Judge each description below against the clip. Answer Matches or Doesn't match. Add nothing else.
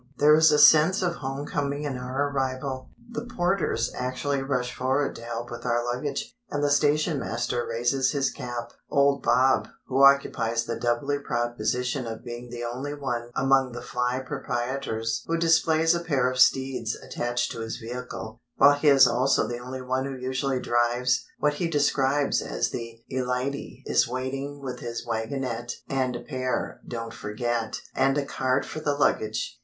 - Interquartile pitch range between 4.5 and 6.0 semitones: Doesn't match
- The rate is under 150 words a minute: Doesn't match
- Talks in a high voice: Doesn't match